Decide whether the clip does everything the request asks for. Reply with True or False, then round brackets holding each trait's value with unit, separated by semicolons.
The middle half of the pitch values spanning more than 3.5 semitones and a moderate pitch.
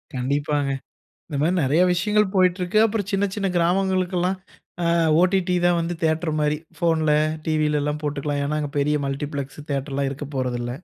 True (4.0 semitones; 155 Hz)